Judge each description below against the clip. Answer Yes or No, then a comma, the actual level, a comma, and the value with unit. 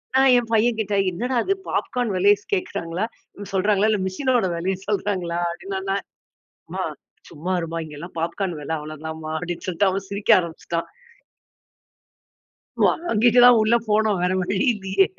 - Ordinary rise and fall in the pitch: Yes, average, 4.2 semitones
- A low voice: No, high, 195 Hz